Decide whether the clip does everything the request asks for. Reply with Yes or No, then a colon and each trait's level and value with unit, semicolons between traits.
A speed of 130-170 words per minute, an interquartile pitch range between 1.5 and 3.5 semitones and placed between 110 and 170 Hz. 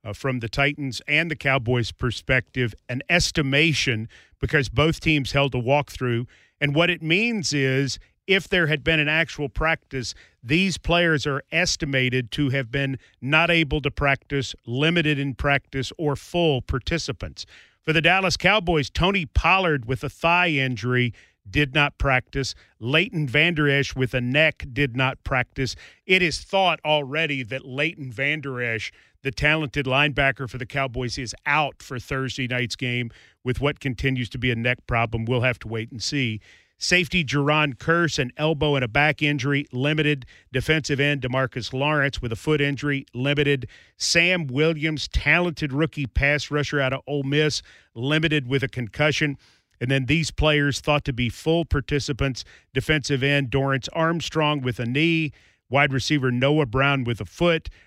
Yes: average, 165 wpm; average, 3.2 semitones; medium, 140 Hz